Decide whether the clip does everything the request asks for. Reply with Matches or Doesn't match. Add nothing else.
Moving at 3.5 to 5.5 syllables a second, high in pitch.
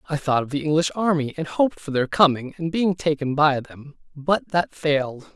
Doesn't match